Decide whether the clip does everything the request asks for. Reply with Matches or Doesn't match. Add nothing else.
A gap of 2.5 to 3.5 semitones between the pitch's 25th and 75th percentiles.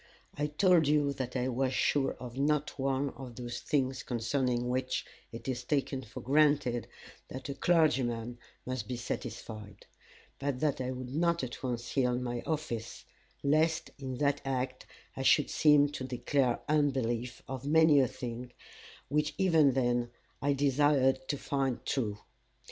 Matches